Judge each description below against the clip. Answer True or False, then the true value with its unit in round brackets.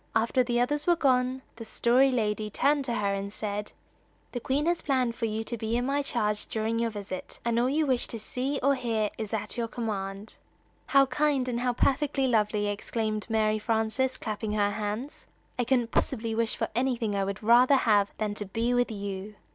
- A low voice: False (230 Hz)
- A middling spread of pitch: True (3.2 semitones)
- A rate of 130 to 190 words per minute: False (205 wpm)